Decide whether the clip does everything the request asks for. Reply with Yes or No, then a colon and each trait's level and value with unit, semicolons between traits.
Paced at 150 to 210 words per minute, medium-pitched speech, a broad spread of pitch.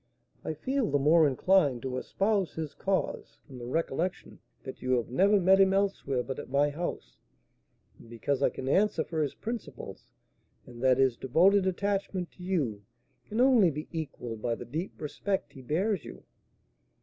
Yes: average, 175 wpm; medium, 160 Hz; wide, 6.6 semitones